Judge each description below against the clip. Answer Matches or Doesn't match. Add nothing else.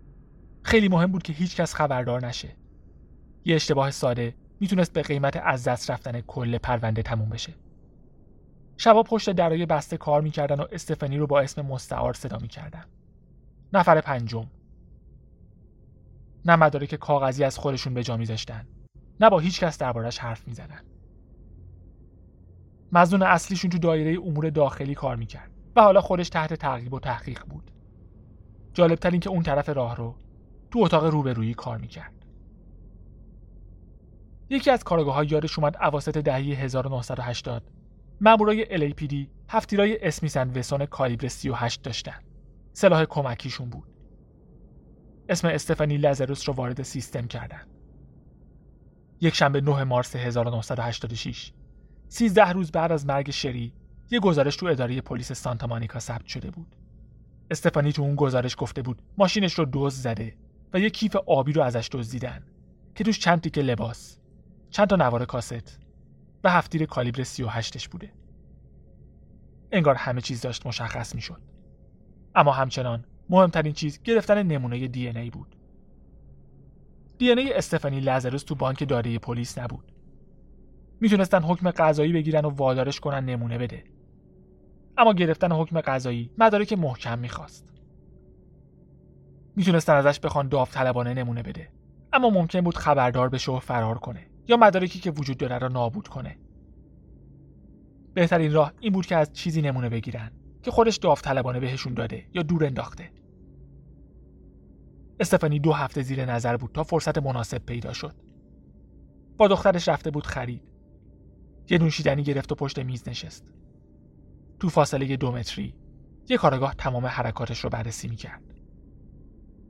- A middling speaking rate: Matches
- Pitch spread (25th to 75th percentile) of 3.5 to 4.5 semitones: Doesn't match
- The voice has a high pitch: Doesn't match